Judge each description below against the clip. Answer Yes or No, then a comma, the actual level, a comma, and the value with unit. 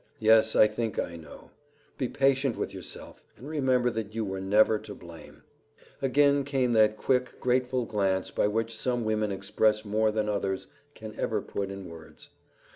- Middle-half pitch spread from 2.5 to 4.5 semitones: Yes, average, 3.7 semitones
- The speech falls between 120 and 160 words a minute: No, average, 170 wpm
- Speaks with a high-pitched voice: No, low, 110 Hz